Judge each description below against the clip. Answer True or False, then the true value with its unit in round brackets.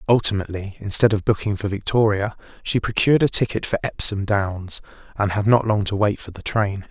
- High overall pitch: False (105 Hz)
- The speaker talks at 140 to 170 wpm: False (190 wpm)